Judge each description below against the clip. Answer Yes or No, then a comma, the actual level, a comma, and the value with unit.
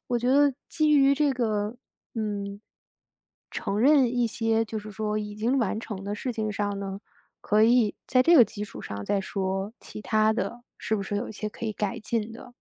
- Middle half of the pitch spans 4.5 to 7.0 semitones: No, average, 2.8 semitones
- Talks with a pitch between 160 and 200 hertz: No, high, 220 Hz